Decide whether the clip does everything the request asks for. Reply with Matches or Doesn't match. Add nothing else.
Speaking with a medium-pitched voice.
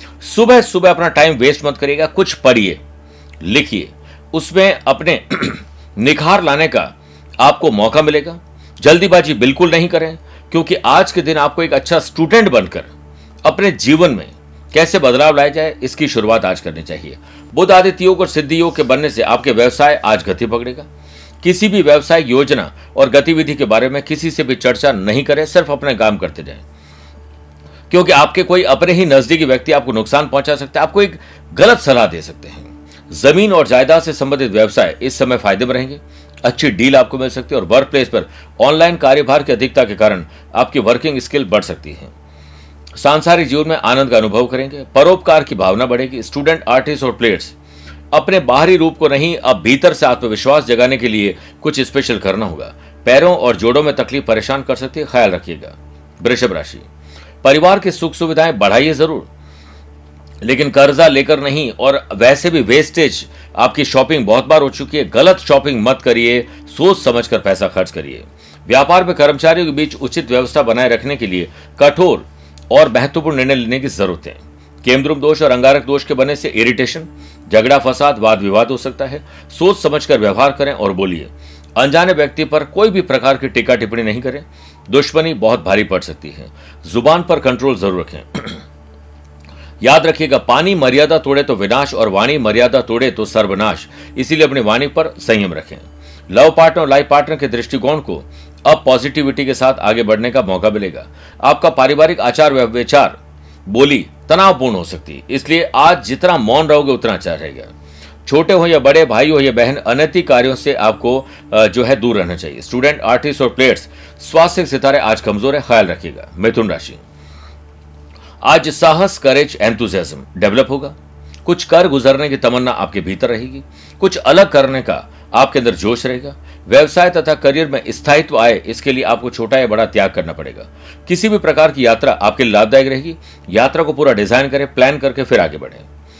Doesn't match